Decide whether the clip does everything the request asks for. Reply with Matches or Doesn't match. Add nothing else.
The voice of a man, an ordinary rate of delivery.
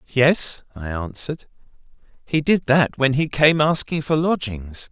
Matches